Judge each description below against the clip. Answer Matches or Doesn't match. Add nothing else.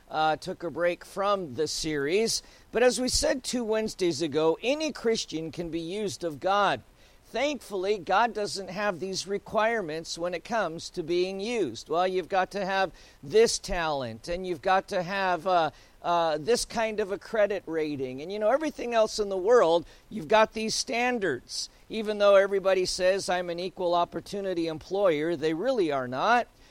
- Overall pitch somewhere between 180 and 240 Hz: Matches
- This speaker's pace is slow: Doesn't match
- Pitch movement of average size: Matches